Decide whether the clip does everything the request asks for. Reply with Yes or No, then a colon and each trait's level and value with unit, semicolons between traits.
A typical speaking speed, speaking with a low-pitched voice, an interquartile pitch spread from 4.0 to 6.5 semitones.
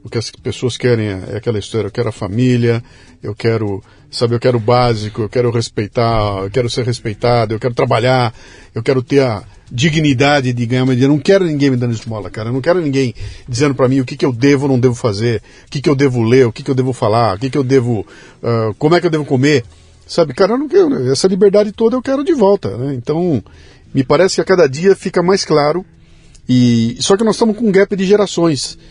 No: fast, 245 wpm; low, 130 Hz; average, 4.7 semitones